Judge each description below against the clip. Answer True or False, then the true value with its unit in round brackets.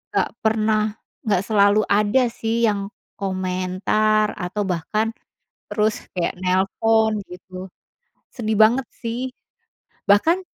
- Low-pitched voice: False (215 Hz)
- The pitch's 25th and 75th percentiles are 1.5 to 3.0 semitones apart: True (2.6 semitones)